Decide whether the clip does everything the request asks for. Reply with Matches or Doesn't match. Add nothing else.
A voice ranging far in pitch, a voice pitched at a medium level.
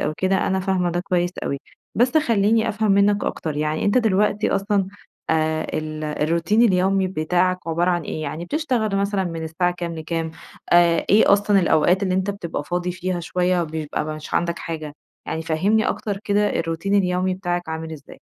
Doesn't match